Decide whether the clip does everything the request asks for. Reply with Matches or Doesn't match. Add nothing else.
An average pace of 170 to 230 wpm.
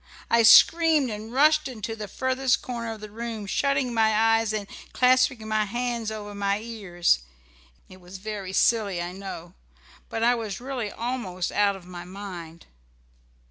Doesn't match